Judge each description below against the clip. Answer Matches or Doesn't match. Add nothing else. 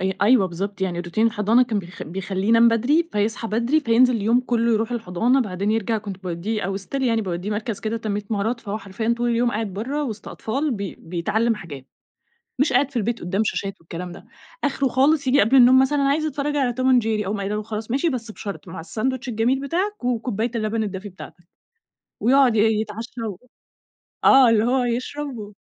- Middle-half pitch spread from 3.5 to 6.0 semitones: Matches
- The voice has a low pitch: Doesn't match